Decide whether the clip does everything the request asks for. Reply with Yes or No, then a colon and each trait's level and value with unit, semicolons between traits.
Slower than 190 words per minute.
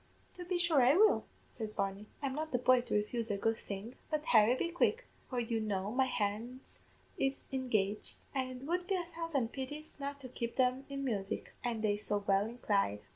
No: fast, 205 wpm